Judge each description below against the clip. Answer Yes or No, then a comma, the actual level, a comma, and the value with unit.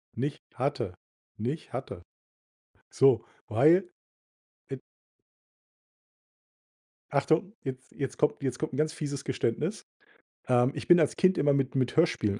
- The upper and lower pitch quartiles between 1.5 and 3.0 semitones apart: No, average, 3.7 semitones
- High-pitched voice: No, low, 135 Hz